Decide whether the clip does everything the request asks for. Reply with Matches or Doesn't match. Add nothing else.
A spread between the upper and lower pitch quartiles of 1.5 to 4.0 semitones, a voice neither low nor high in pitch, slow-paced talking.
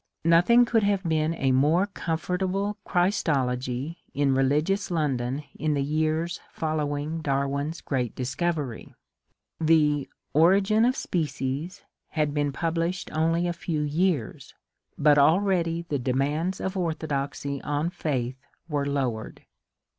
Matches